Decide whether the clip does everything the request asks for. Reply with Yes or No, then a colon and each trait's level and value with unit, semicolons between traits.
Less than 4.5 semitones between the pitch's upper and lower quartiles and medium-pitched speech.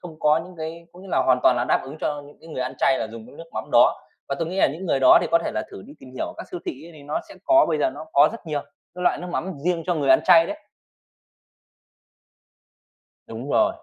Yes: average, 4.1 semitones; medium, 155 Hz